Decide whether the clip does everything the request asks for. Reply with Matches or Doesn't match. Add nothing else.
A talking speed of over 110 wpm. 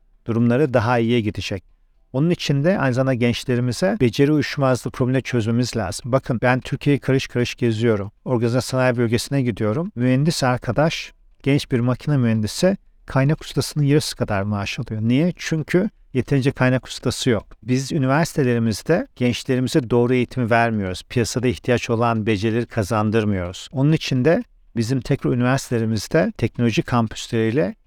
Matches